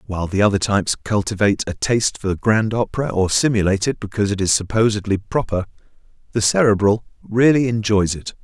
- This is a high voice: No, low, 105 Hz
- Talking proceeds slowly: No, average, 165 wpm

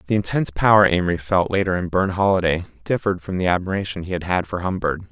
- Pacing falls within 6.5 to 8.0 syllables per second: Yes, 7.0 syllables/s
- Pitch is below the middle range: Yes, very low, 90 Hz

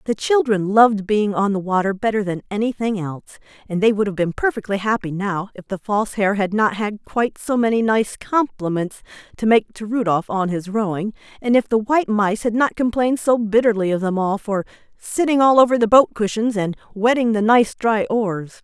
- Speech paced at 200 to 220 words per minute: Yes, fast, 205 wpm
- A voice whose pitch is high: Yes, high, 215 Hz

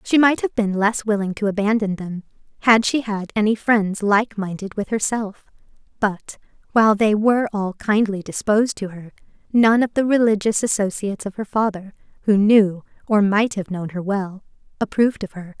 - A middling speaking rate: Yes, average, 175 wpm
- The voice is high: Yes, high, 210 Hz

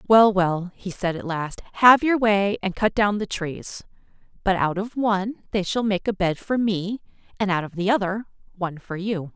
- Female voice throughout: Yes, female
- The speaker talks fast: Yes, fast, 210 wpm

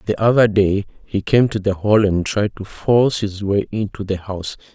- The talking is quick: Yes, fast, 215 wpm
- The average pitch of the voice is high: No, low, 105 Hz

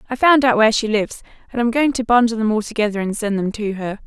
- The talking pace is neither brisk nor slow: No, fast, 280 wpm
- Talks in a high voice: Yes, high, 225 Hz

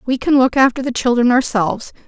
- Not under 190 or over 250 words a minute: Yes, average, 200 wpm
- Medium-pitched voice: No, very high, 250 Hz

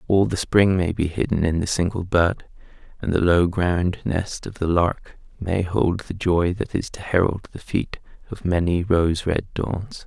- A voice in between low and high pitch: No, very low, 90 Hz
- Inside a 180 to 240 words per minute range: Yes, average, 195 wpm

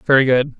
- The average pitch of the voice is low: Yes, low, 130 Hz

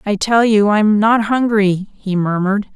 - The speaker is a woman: Yes, female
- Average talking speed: Yes, average, 175 wpm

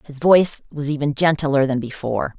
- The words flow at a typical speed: Yes, average, 175 wpm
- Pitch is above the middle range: No, medium, 145 Hz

